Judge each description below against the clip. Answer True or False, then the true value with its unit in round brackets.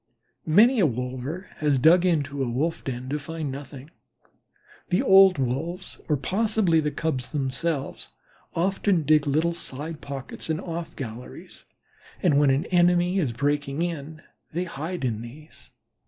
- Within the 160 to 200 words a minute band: False (145 wpm)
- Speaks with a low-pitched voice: False (155 Hz)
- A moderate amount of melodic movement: True (4.1 semitones)